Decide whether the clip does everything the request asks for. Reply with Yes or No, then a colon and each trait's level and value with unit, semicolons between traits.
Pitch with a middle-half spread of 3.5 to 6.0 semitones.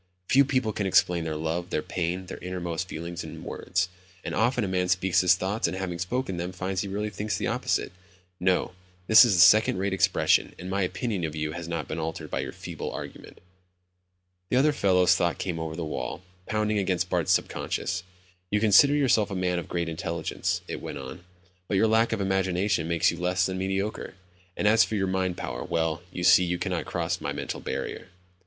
No: average, 2.7 semitones